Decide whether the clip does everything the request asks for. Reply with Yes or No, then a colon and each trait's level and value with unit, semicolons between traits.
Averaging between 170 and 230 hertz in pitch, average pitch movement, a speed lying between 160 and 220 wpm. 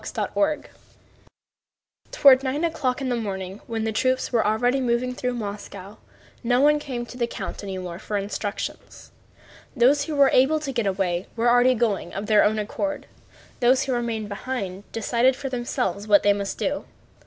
No: high, 240 Hz; average, 4.2 semitones; average, 170 wpm